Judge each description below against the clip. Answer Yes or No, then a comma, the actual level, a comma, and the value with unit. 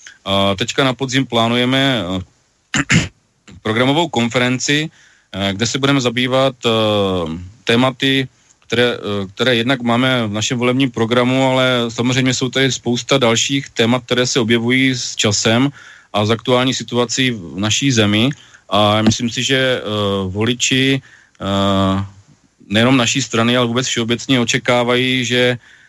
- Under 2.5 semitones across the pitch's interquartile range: No, average, 2.8 semitones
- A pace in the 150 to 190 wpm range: No, average, 120 wpm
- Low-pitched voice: Yes, low, 120 Hz